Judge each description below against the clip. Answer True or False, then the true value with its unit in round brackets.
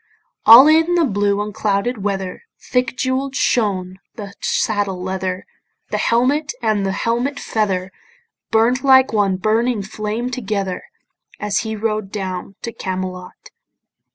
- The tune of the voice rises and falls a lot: False (4.2 semitones)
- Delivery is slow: True (125 wpm)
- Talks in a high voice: True (215 Hz)